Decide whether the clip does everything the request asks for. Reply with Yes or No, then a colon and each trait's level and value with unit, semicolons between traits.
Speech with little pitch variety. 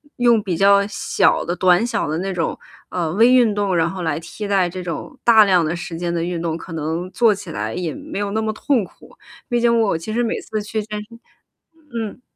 No: average, 4.3 semitones